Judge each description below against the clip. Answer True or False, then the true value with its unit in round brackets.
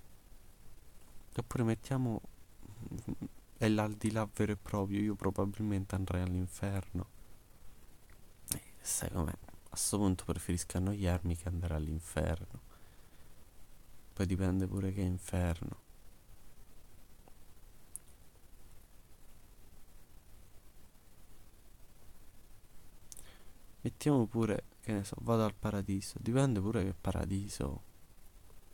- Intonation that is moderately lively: True (3.0 semitones)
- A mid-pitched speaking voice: False (100 Hz)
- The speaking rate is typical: False (90 wpm)